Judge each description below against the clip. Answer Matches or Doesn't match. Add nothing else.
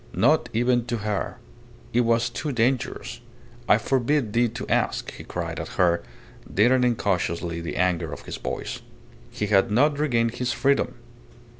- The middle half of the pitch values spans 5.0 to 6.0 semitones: Doesn't match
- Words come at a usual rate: Matches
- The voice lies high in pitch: Doesn't match